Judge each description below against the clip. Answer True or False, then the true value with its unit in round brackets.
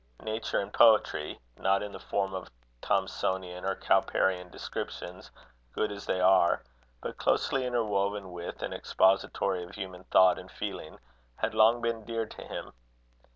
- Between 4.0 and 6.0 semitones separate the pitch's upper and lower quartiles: False (2.9 semitones)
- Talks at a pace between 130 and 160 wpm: True (150 wpm)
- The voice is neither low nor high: False (95 Hz)